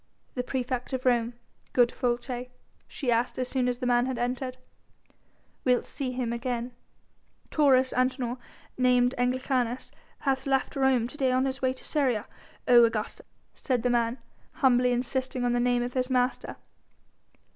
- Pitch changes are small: Yes, narrow, 1.2 semitones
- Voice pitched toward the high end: Yes, very high, 250 Hz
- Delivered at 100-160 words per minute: Yes, average, 155 wpm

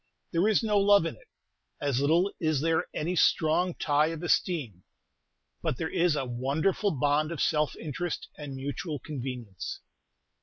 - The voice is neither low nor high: Yes, medium, 155 Hz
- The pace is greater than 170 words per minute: No, average, 155 wpm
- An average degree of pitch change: Yes, average, 3.9 semitones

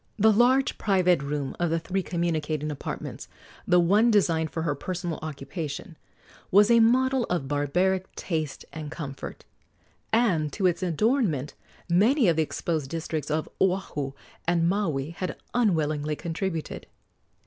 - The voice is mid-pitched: Yes, medium, 170 Hz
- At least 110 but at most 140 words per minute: Yes, slow, 135 wpm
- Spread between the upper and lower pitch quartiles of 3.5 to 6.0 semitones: Yes, average, 4.2 semitones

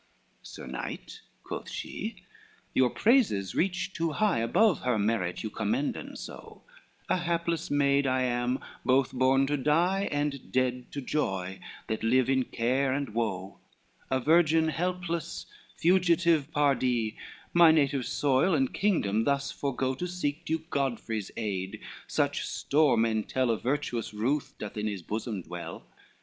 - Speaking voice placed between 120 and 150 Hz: Yes, low, 135 Hz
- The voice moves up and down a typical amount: No, wide, 6.0 semitones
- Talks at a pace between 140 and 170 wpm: Yes, average, 145 wpm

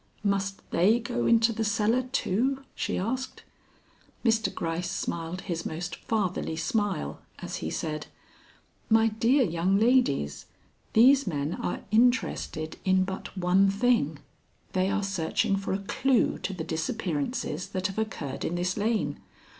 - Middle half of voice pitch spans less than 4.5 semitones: No, average, 4.8 semitones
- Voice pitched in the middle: No, high, 195 Hz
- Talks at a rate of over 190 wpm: No, average, 140 wpm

